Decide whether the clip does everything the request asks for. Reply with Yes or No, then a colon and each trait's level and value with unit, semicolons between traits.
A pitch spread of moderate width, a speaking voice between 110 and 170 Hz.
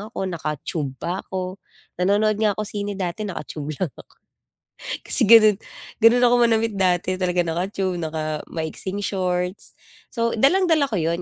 No: average, 3.8 semitones; high, 190 Hz